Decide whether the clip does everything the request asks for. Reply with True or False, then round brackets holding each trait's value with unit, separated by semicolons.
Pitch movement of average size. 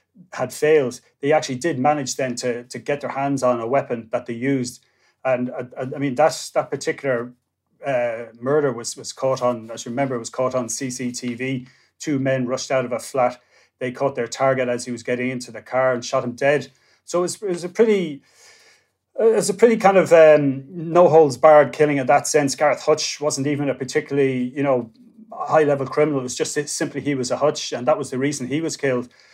True (3.3 semitones)